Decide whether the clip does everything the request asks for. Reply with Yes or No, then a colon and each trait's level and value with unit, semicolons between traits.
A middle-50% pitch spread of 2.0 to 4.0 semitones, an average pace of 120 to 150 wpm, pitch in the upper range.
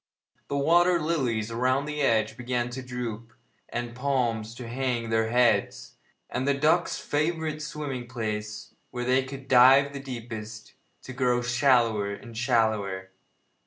No: average, 3.3 semitones; average, 145 wpm; low, 125 Hz